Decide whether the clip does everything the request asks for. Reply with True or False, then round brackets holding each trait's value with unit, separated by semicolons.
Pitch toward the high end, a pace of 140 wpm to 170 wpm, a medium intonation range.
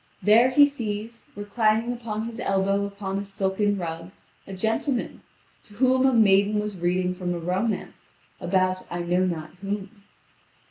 True (200 Hz; 150 wpm; 3.3 semitones)